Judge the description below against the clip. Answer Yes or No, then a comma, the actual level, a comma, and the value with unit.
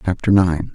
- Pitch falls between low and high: No, very low, 90 Hz